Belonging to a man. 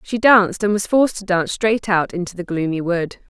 No: female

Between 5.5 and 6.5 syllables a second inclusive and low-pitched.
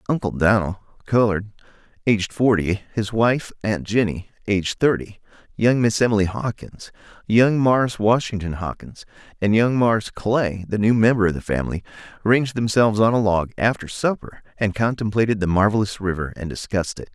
No: 5.2 syllables/s; low, 105 Hz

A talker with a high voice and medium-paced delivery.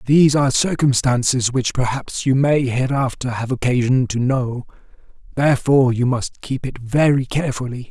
No: low, 130 Hz; average, 145 wpm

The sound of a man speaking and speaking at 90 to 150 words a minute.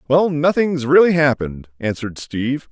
Yes: male; slow, 135 wpm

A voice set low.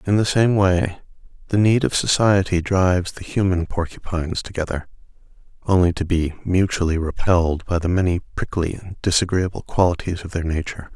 Yes: very low, 90 Hz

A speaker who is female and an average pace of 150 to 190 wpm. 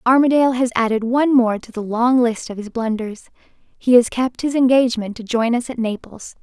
No: female; fast, 205 wpm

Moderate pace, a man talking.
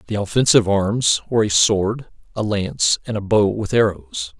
Yes: average, 175 wpm; male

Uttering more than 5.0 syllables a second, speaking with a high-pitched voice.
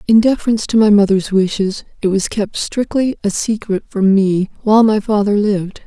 Yes: 5.3 syllables/s; high, 205 Hz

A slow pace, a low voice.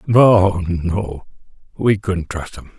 Yes: slow, 110 wpm; very low, 95 Hz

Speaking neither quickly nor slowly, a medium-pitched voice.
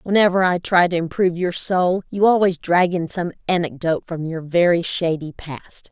Yes: average, 185 wpm; medium, 175 Hz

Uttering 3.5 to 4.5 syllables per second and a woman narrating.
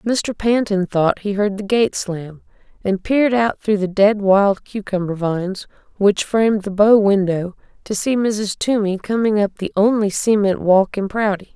Yes: 4.4 syllables/s; female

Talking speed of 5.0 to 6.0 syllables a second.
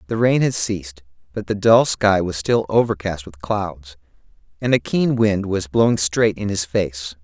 No: 4.4 syllables/s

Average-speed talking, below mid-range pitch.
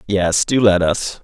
Yes: average, 195 wpm; low, 100 Hz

